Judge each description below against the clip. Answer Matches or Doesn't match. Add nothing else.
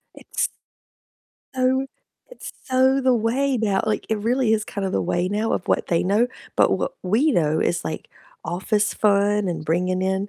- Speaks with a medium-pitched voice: Doesn't match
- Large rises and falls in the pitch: Doesn't match